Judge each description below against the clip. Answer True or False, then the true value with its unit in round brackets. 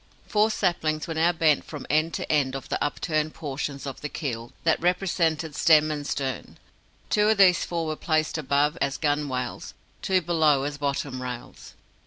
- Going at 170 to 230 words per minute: True (175 wpm)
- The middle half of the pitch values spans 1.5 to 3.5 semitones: True (2.8 semitones)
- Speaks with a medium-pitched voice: True (155 Hz)